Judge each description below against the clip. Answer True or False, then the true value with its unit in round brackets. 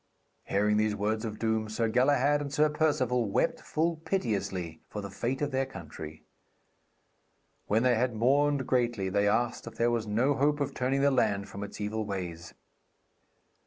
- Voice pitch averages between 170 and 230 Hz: False (115 Hz)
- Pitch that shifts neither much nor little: True (4.6 semitones)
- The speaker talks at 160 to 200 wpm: True (170 wpm)